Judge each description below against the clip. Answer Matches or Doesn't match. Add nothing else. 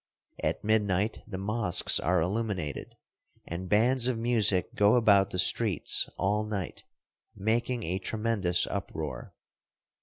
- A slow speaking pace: Matches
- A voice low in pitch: Matches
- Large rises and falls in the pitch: Doesn't match